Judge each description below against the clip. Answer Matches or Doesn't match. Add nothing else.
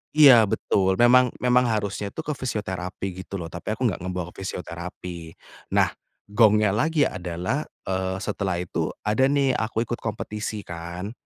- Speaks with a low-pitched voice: Matches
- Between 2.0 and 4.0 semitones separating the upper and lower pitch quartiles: Doesn't match